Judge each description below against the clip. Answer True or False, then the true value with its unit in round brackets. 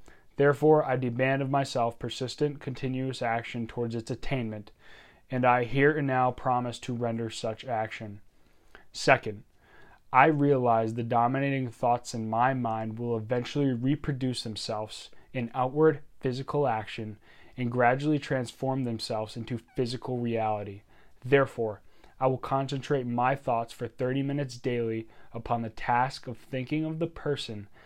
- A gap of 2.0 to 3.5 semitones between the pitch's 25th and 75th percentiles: True (2.8 semitones)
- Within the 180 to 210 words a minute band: False (135 wpm)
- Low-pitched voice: True (125 Hz)